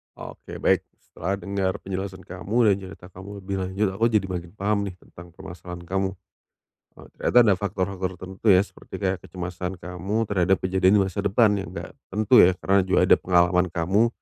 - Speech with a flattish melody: Yes, narrow, 1.6 semitones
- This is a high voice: No, very low, 95 Hz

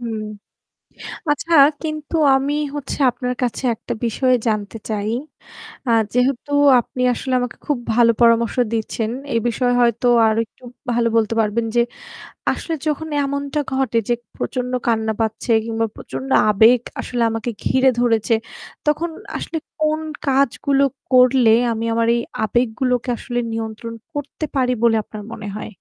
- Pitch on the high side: Yes, high, 240 Hz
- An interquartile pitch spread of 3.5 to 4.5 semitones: No, average, 3.0 semitones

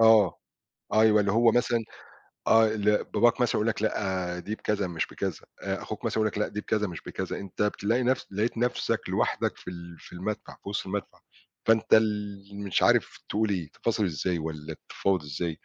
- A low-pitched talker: Yes, low, 105 Hz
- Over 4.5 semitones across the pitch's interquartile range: No, average, 3.1 semitones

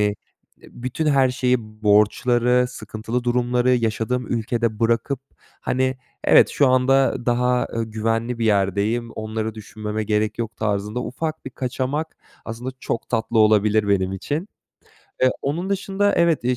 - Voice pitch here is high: No, low, 120 Hz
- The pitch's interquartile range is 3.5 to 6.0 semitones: No, average, 2.8 semitones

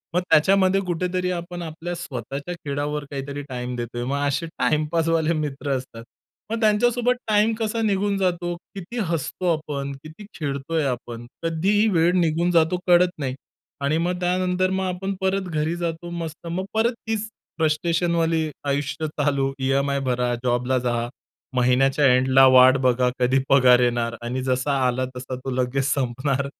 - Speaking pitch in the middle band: Yes, medium, 155 Hz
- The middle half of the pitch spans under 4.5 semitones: No, average, 5.2 semitones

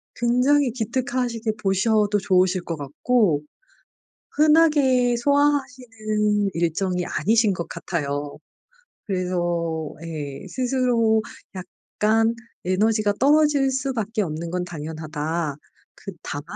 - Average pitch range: No, wide, 6.4 semitones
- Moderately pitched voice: No, high, 210 Hz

